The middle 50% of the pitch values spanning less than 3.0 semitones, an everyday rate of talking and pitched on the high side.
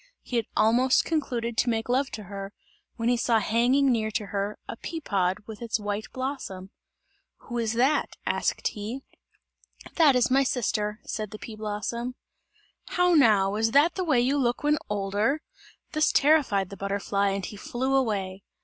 No: average, 4.2 semitones; average, 175 wpm; high, 230 Hz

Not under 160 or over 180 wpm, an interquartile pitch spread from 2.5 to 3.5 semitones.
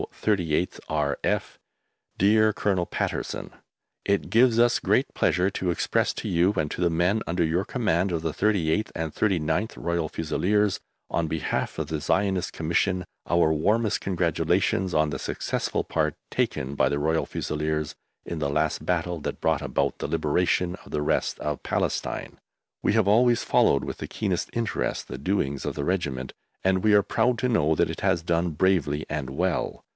No: average, 170 wpm; average, 4.3 semitones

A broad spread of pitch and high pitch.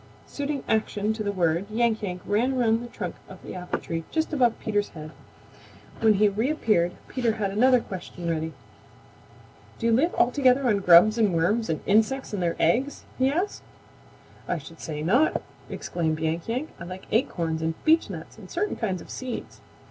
Yes: wide, 6.0 semitones; high, 215 Hz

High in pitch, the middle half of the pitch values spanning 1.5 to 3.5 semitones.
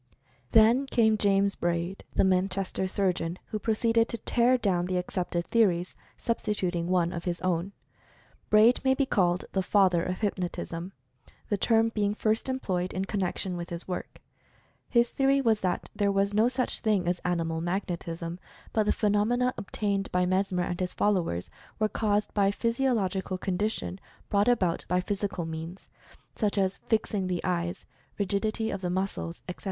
Yes: high, 195 Hz; average, 3.2 semitones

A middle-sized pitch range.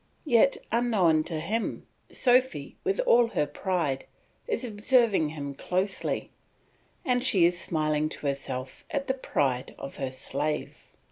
No: wide, 8.6 semitones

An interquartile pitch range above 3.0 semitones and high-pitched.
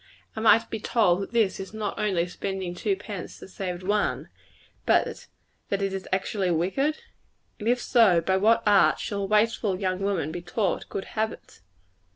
No: average, 2.7 semitones; high, 195 Hz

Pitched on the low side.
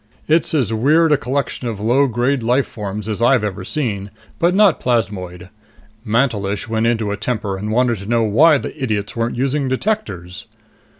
Yes: low, 115 Hz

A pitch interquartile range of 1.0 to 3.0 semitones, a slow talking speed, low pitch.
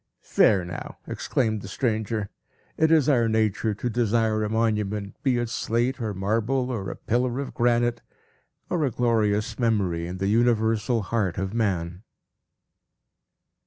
No: average, 2.7 semitones; average, 145 wpm; low, 110 Hz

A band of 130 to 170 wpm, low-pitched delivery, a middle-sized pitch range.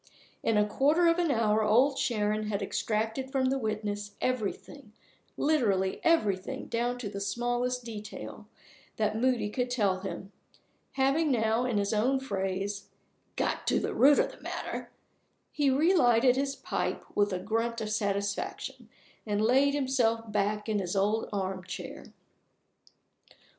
No: average, 140 wpm; high, 220 Hz; average, 4.0 semitones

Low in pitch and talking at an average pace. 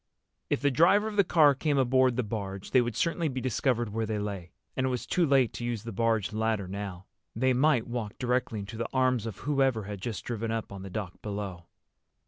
No: low, 115 Hz; fast, 225 wpm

